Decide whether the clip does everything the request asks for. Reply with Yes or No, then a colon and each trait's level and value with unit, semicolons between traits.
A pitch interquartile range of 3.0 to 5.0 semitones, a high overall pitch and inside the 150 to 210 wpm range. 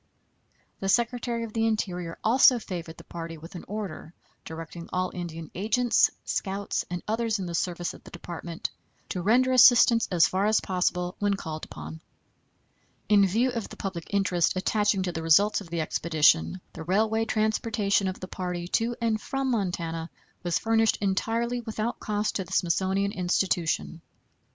Yes: average, 4.2 semitones; high, 195 Hz; average, 165 wpm